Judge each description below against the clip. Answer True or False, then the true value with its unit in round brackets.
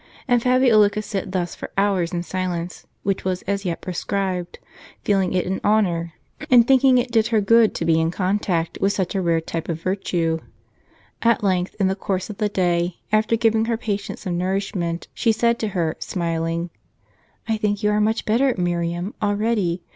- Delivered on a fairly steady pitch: False (3.7 semitones)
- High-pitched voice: True (195 Hz)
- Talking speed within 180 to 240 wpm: True (185 wpm)